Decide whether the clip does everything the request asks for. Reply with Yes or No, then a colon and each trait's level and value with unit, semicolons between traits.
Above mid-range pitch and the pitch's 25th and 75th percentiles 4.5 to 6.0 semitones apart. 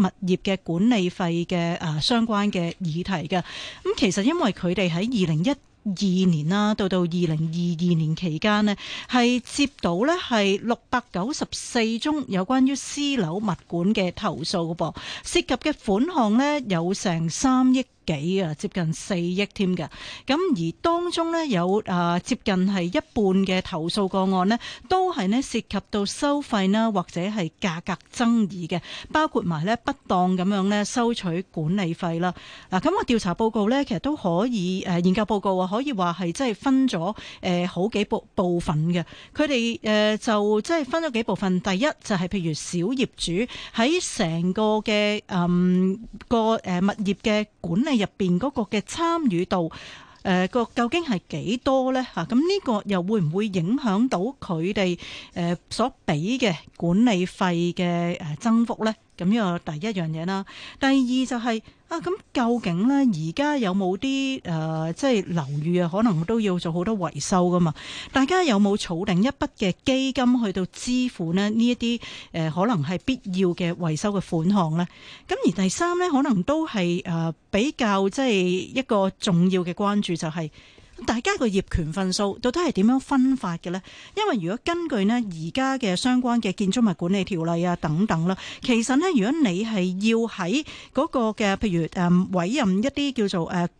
Yes: high, 200 Hz; average, 5.3 semitones